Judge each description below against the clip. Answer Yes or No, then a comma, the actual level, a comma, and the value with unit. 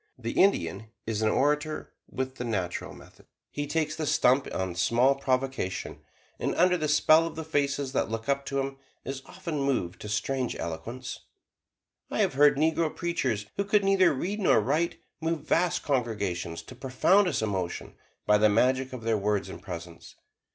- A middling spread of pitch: No, wide, 5.9 semitones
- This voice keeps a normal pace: Yes, average, 170 wpm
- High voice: No, low, 135 Hz